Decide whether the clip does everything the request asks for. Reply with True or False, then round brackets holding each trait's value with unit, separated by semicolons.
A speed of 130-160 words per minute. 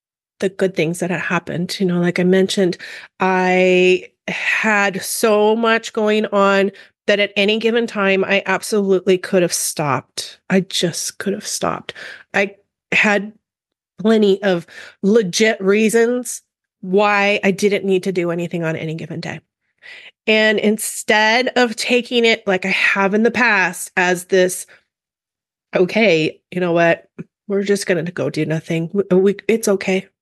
True (150 wpm)